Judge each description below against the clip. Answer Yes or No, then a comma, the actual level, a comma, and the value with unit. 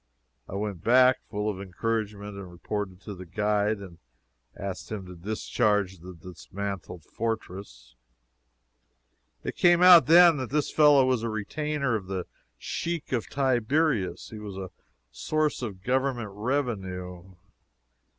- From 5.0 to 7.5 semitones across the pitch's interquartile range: Yes, wide, 5.4 semitones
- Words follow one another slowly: Yes, slow, 130 wpm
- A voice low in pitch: Yes, low, 105 Hz